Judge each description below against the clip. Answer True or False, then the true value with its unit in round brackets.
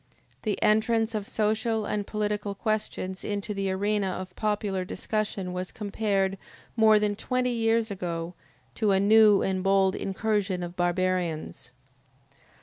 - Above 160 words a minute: False (135 wpm)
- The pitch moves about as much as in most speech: False (2.3 semitones)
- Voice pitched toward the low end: False (205 Hz)